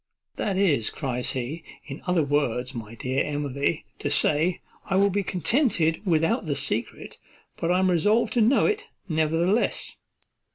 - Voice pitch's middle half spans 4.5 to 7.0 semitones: Yes, average, 5.2 semitones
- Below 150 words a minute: No, average, 155 wpm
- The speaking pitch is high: No, medium, 160 Hz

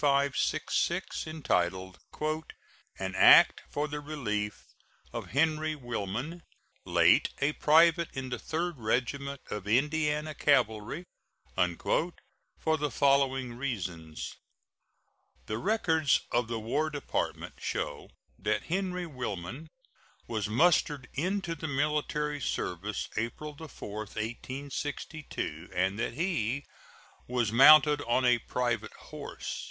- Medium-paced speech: No, slow, 105 wpm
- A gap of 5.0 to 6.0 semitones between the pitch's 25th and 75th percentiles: Yes, wide, 5.6 semitones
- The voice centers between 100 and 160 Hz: Yes, medium, 140 Hz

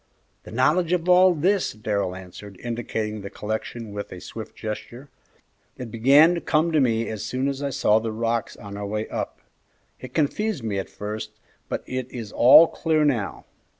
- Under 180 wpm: No, average, 185 wpm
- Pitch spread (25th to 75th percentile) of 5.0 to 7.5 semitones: Yes, wide, 5.5 semitones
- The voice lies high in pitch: No, low, 115 Hz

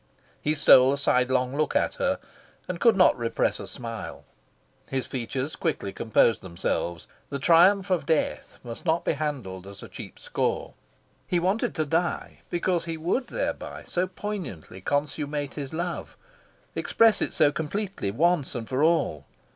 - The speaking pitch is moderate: Yes, medium, 150 Hz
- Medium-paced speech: Yes, average, 155 wpm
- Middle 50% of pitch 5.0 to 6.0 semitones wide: Yes, wide, 5.5 semitones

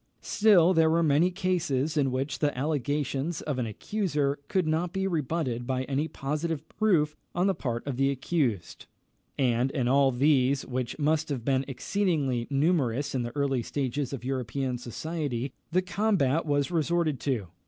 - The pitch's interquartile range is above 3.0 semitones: Yes, average, 3.8 semitones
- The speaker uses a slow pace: No, average, 165 wpm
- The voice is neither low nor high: Yes, medium, 145 Hz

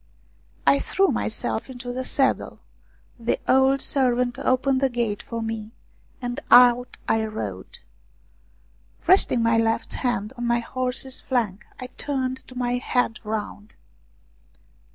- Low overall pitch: No, high, 245 Hz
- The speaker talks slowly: Yes, slow, 125 wpm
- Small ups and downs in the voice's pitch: Yes, narrow, 2.2 semitones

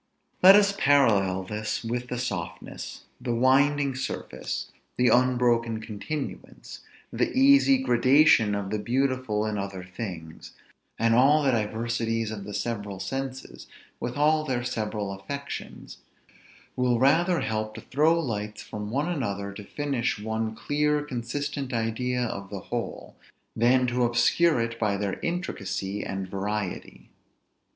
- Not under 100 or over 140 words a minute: Yes, slow, 135 wpm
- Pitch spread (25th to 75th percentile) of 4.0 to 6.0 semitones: Yes, average, 4.6 semitones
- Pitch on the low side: Yes, low, 120 Hz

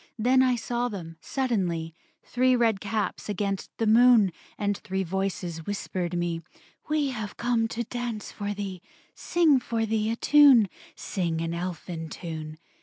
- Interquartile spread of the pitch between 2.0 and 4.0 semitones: No, average, 5.3 semitones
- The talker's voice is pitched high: Yes, high, 205 Hz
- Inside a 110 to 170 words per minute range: Yes, average, 150 wpm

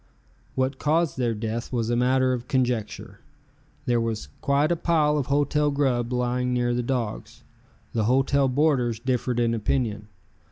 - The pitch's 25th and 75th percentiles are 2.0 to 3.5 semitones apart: Yes, average, 2.9 semitones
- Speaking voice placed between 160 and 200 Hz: No, low, 125 Hz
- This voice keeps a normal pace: Yes, average, 155 wpm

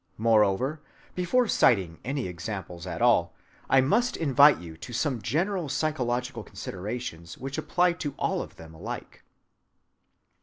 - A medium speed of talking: No, slow, 130 wpm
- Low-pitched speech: Yes, low, 125 Hz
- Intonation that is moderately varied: No, wide, 7.8 semitones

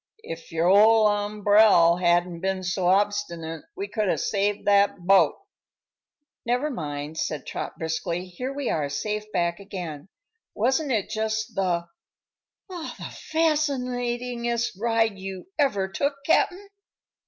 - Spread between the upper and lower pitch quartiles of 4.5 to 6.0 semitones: Yes, average, 5.3 semitones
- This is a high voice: Yes, high, 205 Hz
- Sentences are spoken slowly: Yes, slow, 125 wpm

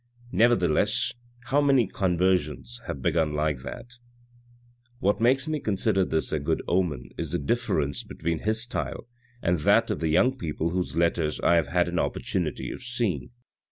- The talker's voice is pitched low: Yes, very low, 90 Hz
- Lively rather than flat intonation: Yes, wide, 7.0 semitones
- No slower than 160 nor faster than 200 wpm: Yes, average, 165 wpm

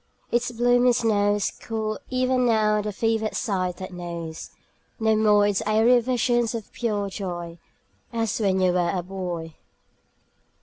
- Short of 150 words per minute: Yes, average, 140 wpm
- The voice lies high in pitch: Yes, high, 215 Hz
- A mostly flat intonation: No, average, 3.7 semitones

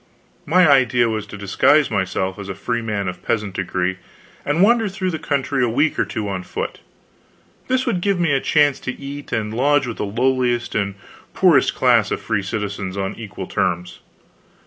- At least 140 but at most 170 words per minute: No, average, 185 wpm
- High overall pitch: No, low, 115 Hz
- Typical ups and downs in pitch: No, wide, 6.5 semitones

